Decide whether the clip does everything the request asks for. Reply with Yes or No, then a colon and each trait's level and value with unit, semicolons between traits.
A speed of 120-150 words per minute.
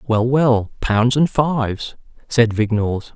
Yes: slow, 135 wpm